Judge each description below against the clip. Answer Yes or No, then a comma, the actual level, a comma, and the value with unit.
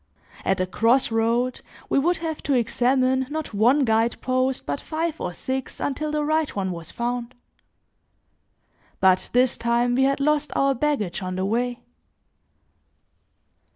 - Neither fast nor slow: Yes, average, 150 wpm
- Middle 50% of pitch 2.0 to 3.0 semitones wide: No, average, 3.7 semitones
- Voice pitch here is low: No, very high, 250 Hz